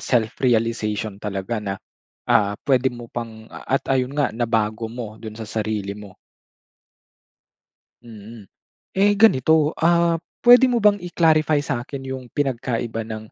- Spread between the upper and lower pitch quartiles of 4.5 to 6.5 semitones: Yes, average, 4.9 semitones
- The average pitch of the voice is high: No, low, 120 Hz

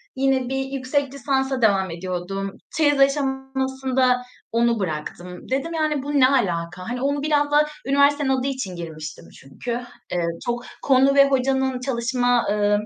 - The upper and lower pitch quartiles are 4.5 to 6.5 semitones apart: Yes, average, 4.8 semitones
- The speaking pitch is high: Yes, very high, 260 Hz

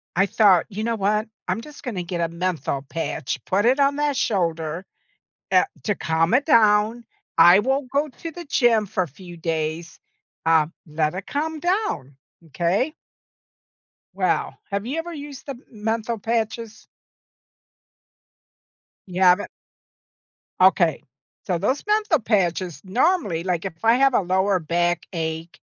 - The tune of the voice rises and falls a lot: Yes, wide, 6.4 semitones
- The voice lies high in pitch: Yes, high, 200 Hz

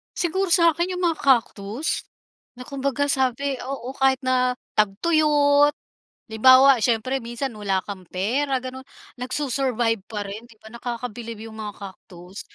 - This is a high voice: Yes, very high, 255 Hz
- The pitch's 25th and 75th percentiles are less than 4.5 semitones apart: Yes, average, 4.1 semitones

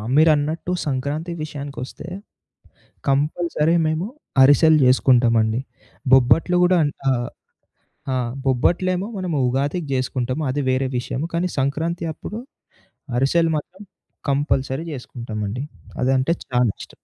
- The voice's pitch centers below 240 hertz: Yes, medium, 140 Hz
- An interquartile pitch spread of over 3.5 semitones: Yes, average, 4.1 semitones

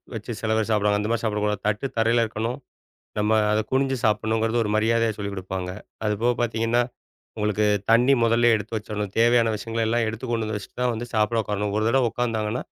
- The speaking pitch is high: No, low, 110 Hz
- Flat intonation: Yes, narrow, 1.7 semitones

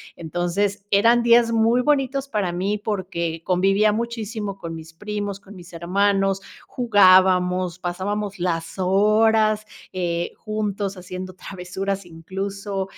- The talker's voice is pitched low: No, high, 195 Hz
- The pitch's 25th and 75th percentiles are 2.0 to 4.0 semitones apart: Yes, average, 2.7 semitones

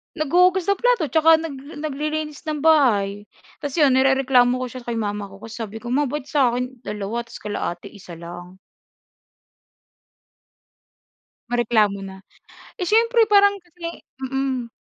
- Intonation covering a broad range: Yes, wide, 6.1 semitones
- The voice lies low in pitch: No, very high, 260 Hz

